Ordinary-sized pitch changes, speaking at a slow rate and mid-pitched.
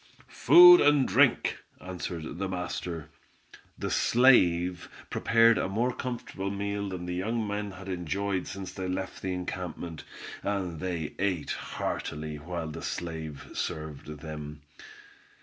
No: average, 3.6 semitones; slow, 130 wpm; very low, 90 Hz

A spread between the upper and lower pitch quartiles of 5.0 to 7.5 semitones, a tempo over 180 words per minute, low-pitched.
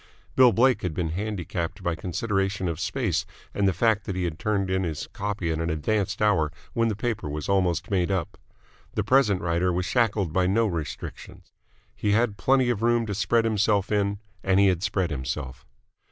No: average, 3.6 semitones; average, 195 wpm; very low, 95 Hz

